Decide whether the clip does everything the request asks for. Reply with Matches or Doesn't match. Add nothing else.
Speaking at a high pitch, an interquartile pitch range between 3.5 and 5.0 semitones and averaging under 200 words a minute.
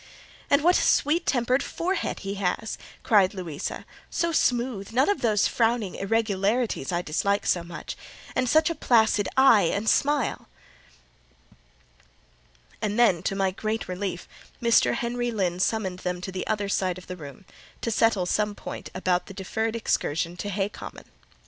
Matches